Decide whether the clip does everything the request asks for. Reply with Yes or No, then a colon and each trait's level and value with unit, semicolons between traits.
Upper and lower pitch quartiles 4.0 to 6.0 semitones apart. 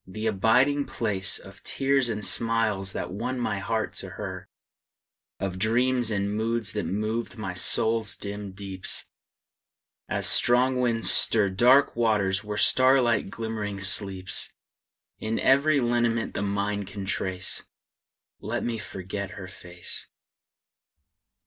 No: average, 3.2 semitones